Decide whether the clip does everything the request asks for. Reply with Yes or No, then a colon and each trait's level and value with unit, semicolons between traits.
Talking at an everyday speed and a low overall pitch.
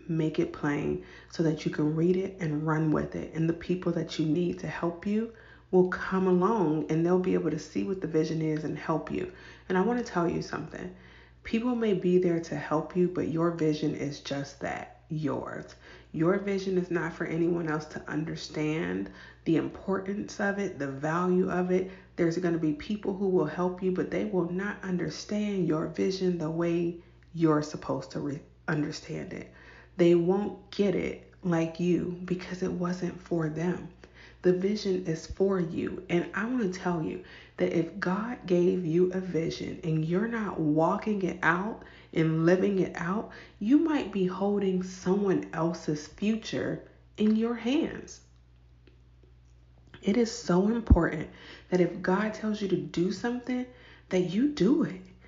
No: average, 180 wpm; medium, 175 Hz